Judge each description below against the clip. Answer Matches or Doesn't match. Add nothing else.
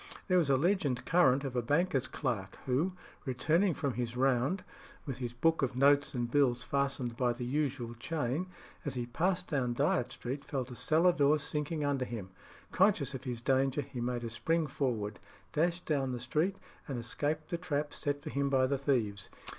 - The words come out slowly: Doesn't match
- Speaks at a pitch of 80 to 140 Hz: Matches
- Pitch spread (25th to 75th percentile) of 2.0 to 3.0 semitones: Doesn't match